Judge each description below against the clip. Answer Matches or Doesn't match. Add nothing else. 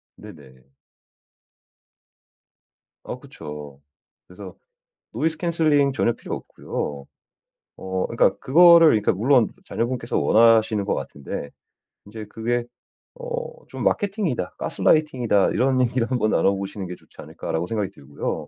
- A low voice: Matches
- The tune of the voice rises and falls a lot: Matches